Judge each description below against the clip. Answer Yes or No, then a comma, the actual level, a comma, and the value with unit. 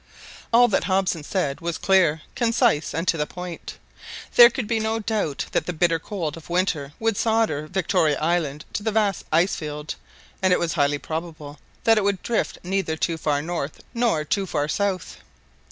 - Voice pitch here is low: No, medium, 175 Hz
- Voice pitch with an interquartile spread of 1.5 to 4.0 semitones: No, average, 4.9 semitones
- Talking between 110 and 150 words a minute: No, average, 185 wpm